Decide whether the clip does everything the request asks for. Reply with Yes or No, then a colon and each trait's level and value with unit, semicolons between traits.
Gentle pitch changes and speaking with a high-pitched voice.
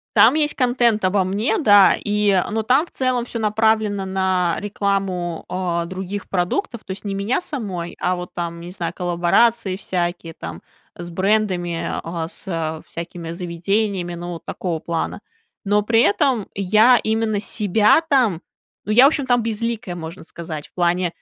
No: average, 4.0 semitones; high, 195 Hz